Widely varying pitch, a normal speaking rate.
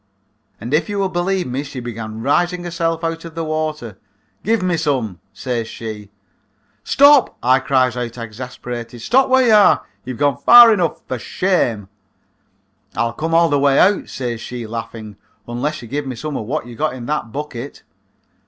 Yes: wide, 5.9 semitones; average, 180 wpm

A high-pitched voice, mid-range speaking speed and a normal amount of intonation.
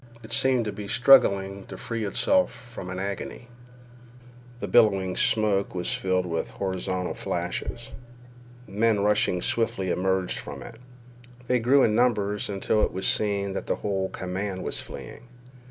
No: low, 100 Hz; average, 150 wpm; average, 3.2 semitones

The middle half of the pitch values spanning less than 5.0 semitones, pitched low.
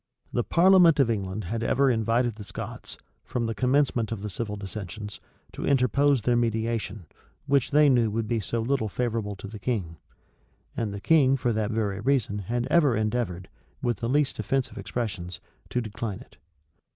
Yes: average, 3.5 semitones; low, 115 Hz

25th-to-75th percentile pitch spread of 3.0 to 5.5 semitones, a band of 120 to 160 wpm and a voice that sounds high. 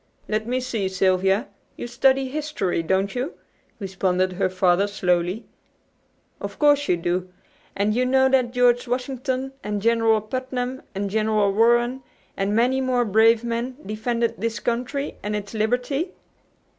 Yes: average, 4.2 semitones; average, 145 wpm; high, 230 Hz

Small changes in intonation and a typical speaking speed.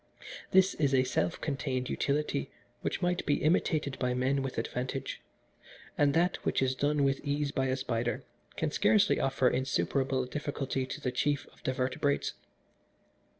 Yes: narrow, 2.1 semitones; average, 155 wpm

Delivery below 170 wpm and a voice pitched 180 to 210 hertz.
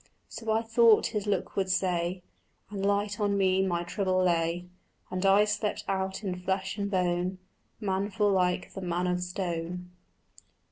Yes: average, 155 wpm; high, 190 Hz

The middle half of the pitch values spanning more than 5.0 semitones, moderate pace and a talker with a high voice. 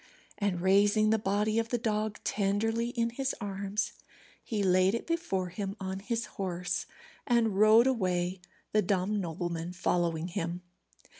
No: average, 3.3 semitones; average, 145 wpm; high, 200 Hz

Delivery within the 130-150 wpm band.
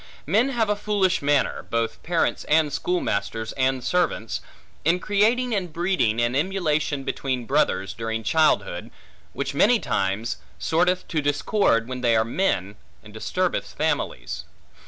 Yes: slow, 135 wpm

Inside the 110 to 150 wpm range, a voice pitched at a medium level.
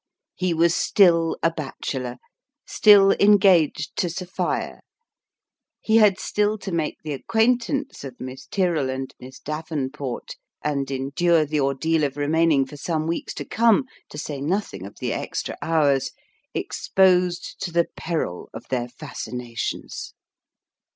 Yes: average, 140 wpm; medium, 160 Hz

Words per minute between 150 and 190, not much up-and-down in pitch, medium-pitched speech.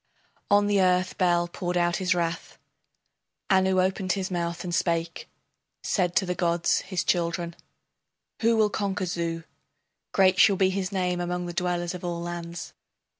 Yes: average, 160 wpm; narrow, 1.6 semitones; medium, 180 Hz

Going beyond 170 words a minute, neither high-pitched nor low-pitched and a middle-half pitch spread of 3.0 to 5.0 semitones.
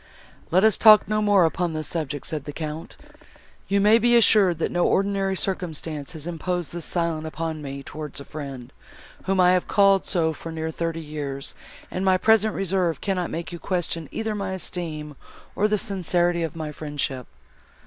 Yes: average, 180 wpm; medium, 170 Hz; average, 3.7 semitones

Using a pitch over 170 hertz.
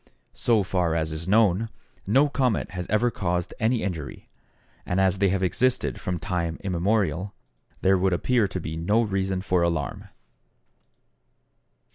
No: very low, 95 Hz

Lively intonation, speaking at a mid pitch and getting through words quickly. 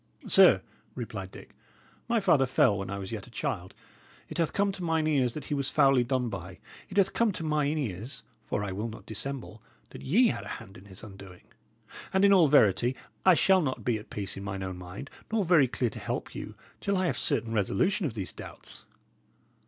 No: wide, 8.3 semitones; low, 130 Hz; fast, 215 wpm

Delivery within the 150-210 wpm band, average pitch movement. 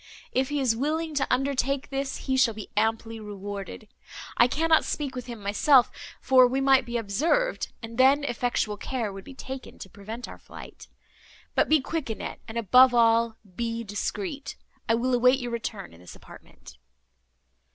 Yes: average, 170 wpm; average, 3.3 semitones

